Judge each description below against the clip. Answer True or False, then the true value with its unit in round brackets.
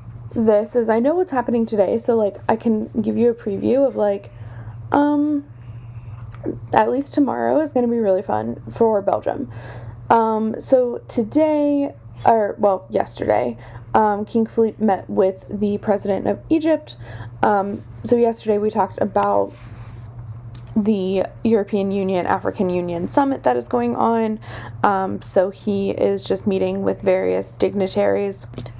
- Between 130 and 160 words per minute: True (145 wpm)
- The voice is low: False (200 Hz)